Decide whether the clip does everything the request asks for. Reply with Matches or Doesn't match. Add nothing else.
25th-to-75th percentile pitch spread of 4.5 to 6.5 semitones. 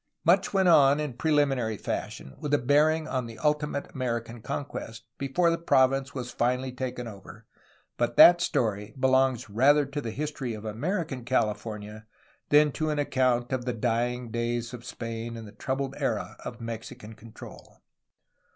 Doesn't match